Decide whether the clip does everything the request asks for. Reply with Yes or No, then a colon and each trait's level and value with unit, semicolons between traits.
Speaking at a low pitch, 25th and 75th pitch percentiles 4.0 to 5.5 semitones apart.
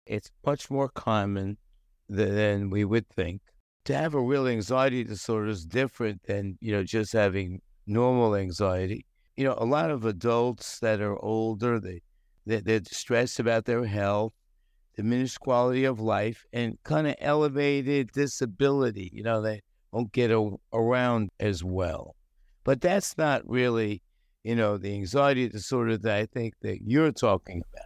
No: low, 110 Hz; average, 3.6 semitones